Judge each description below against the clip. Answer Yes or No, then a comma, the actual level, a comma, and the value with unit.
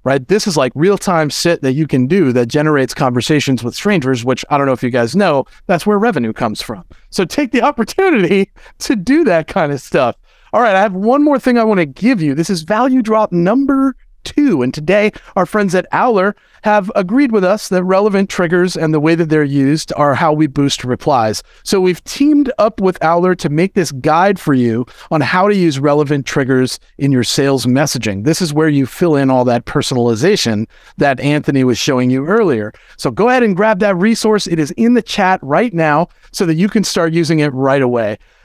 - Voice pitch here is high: No, medium, 170 Hz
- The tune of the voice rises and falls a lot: Yes, wide, 7.0 semitones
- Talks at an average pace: No, fast, 220 wpm